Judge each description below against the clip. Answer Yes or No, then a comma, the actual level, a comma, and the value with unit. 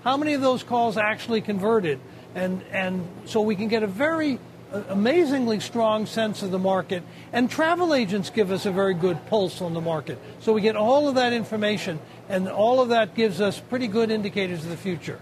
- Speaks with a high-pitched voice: Yes, high, 215 Hz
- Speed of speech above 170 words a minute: Yes, fast, 205 wpm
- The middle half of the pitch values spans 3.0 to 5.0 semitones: Yes, average, 3.8 semitones